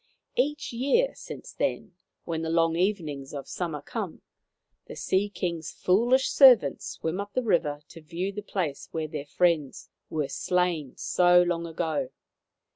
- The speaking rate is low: No, average, 150 wpm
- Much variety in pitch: No, average, 4.5 semitones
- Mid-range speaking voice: Yes, medium, 170 Hz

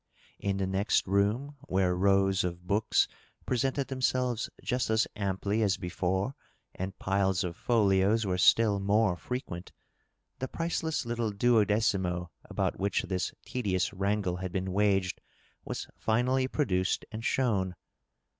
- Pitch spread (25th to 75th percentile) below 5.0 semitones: Yes, average, 3.5 semitones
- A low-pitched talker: Yes, low, 100 Hz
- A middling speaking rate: No, slow, 130 wpm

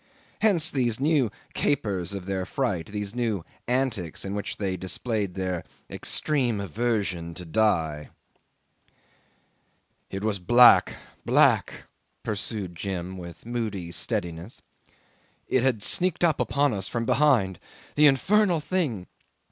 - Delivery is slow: Yes, slow, 115 wpm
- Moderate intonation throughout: No, wide, 5.8 semitones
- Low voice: Yes, low, 105 Hz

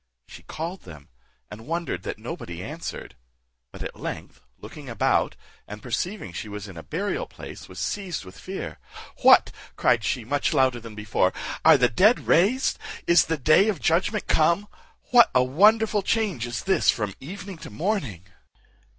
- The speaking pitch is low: No, medium, 155 Hz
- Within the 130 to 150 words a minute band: No, average, 165 wpm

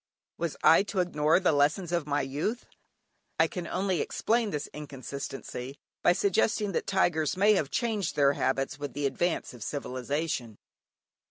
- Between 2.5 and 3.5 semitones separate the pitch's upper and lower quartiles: No, average, 5.1 semitones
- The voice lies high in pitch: No, medium, 155 Hz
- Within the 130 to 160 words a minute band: Yes, average, 155 wpm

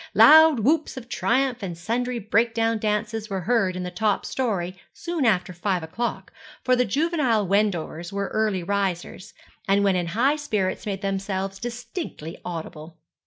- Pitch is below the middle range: No, high, 210 Hz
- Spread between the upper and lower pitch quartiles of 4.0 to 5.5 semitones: Yes, average, 4.5 semitones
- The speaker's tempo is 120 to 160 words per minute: Yes, average, 155 wpm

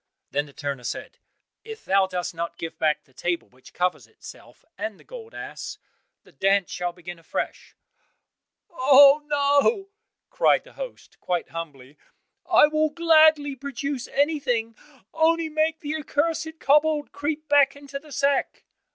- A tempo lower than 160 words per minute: Yes, average, 145 wpm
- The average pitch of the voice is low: No, very high, 280 Hz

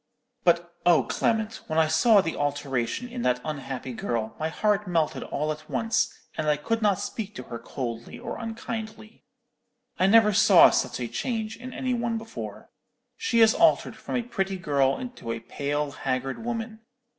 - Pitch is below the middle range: No, medium, 185 Hz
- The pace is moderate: Yes, average, 175 wpm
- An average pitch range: No, wide, 7.8 semitones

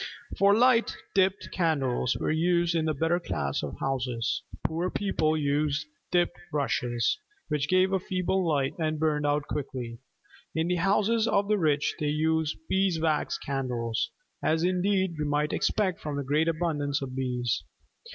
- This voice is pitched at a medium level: Yes, medium, 155 Hz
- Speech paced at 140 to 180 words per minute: Yes, average, 155 wpm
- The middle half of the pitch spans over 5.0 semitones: No, average, 4.1 semitones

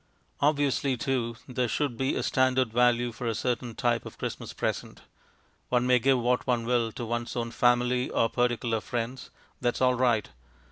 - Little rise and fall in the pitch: Yes, narrow, 1.3 semitones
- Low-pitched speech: Yes, low, 125 Hz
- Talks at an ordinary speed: Yes, average, 180 wpm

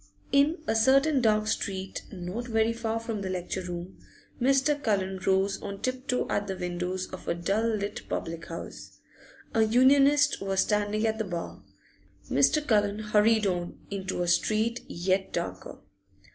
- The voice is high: Yes, high, 210 Hz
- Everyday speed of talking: Yes, average, 160 wpm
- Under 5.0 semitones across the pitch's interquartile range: Yes, average, 3.5 semitones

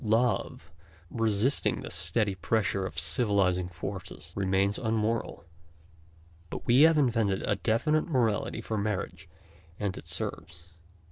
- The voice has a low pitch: Yes, low, 105 Hz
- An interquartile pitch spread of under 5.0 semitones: Yes, average, 3.4 semitones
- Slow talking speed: Yes, slow, 125 wpm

